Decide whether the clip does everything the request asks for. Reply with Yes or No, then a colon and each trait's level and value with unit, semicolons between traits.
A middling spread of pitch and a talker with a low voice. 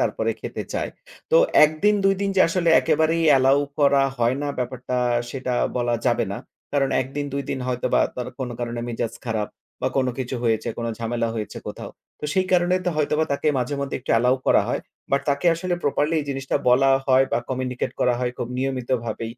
Yes: average, 3.1 semitones; low, 130 Hz